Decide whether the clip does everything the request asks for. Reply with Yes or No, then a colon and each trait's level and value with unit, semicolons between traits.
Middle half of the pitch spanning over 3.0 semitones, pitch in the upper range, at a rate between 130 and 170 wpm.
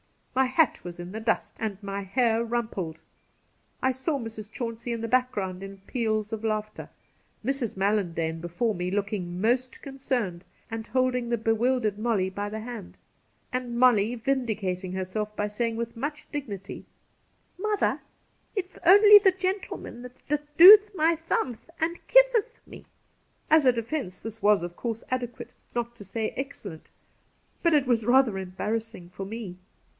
Yes: average, 4.4 semitones; high, 230 Hz; average, 155 wpm